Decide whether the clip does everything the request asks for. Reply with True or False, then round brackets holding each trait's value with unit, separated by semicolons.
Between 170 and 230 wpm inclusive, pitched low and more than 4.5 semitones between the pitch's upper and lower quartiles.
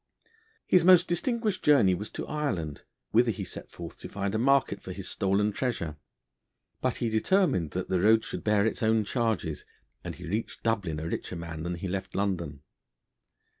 True (180 wpm; 100 Hz; 5.0 semitones)